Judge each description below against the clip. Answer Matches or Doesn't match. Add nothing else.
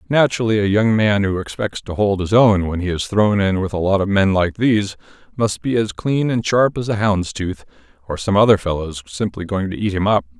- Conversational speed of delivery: Doesn't match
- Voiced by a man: Matches